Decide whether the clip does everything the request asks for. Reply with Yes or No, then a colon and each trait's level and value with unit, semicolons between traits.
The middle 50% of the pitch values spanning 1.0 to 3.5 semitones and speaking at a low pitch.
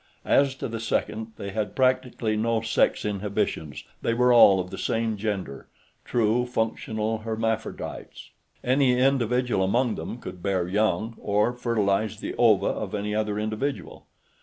Yes: average, 2.7 semitones; low, 110 Hz